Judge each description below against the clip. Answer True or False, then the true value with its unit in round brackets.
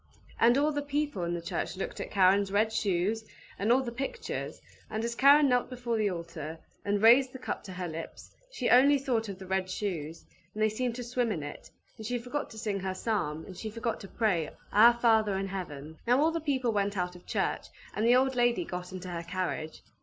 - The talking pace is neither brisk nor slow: False (230 wpm)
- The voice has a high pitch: True (215 Hz)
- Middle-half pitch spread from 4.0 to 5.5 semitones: True (5.1 semitones)